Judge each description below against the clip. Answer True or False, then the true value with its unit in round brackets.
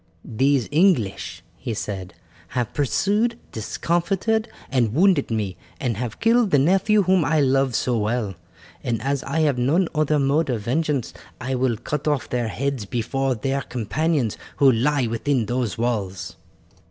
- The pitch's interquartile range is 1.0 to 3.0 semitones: False (5.0 semitones)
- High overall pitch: False (135 Hz)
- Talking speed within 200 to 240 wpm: False (155 wpm)